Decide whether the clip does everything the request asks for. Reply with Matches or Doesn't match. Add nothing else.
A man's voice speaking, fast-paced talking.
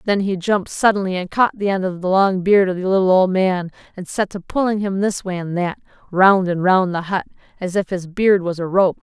Doesn't match